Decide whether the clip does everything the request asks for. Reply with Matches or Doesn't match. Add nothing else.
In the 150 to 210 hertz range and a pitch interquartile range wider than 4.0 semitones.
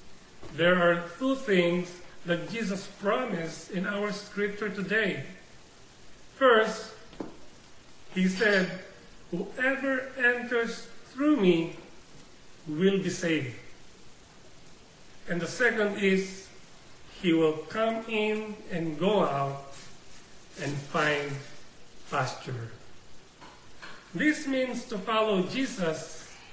Matches